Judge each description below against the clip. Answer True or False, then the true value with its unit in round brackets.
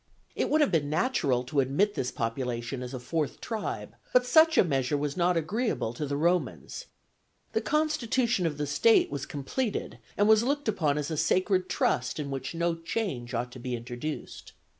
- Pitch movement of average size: False (8.1 semitones)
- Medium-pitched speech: True (155 Hz)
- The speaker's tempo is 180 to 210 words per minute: True (185 wpm)